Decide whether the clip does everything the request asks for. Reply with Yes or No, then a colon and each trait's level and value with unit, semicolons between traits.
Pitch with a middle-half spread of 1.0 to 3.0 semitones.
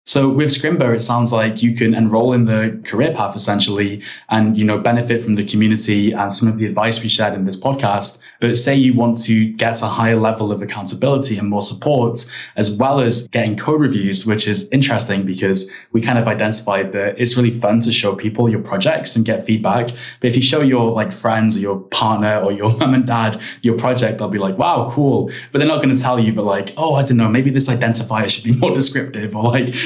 Yes: narrow, 2.5 semitones